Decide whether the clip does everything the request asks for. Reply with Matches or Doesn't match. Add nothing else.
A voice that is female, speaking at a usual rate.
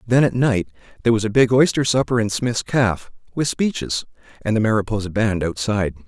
Doesn't match